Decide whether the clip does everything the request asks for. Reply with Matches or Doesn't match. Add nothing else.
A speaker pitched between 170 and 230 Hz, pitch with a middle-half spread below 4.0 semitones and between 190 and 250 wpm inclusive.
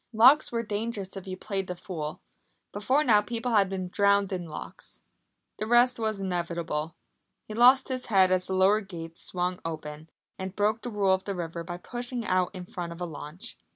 Matches